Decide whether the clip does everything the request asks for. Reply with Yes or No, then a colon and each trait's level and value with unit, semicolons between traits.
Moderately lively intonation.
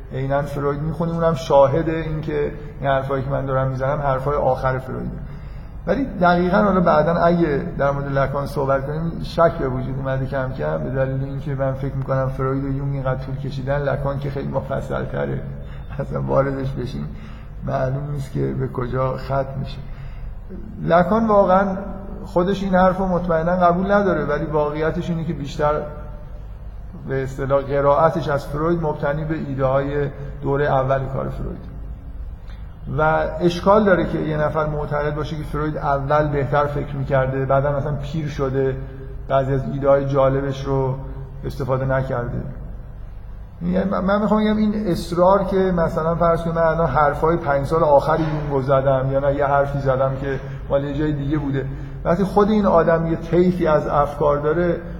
Yes: average, 3.3 semitones